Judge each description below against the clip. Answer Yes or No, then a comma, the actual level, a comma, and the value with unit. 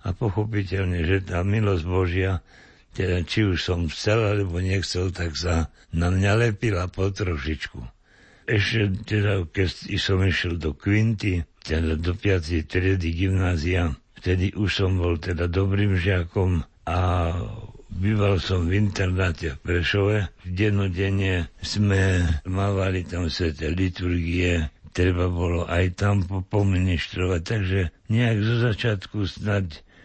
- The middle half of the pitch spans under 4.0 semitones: Yes, narrow, 2.4 semitones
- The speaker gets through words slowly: No, average, 125 wpm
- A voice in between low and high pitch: No, very low, 95 Hz